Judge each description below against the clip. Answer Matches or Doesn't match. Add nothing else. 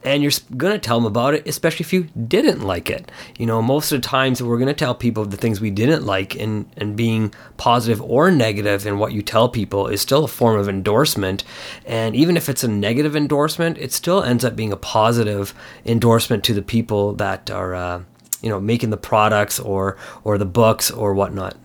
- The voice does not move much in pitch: Doesn't match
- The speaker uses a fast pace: Matches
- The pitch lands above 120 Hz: Doesn't match